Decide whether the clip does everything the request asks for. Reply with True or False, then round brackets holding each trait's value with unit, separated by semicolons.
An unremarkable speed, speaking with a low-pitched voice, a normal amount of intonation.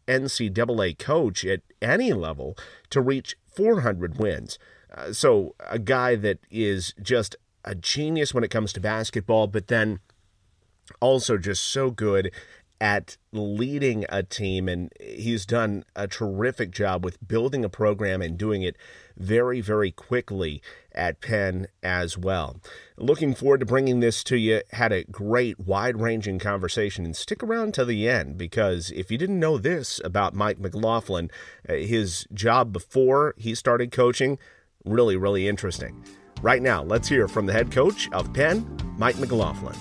True (150 wpm; 110 Hz; 4.0 semitones)